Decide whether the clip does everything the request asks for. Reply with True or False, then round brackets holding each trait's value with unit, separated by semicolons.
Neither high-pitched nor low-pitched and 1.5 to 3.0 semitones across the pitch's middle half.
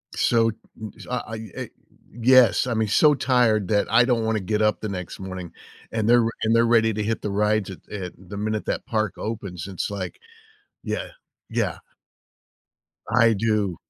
False (110 Hz; 2.4 semitones)